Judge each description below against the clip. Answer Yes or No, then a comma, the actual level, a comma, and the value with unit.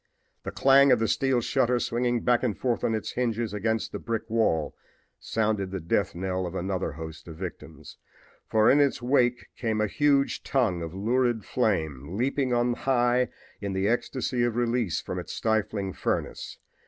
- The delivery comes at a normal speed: Yes, average, 165 wpm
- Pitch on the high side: No, low, 115 Hz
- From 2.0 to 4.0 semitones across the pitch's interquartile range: No, average, 4.4 semitones